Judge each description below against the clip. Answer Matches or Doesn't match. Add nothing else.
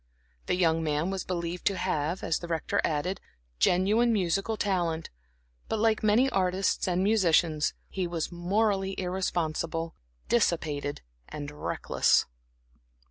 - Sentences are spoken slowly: Matches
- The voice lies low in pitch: Doesn't match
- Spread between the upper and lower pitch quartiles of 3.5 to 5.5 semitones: Doesn't match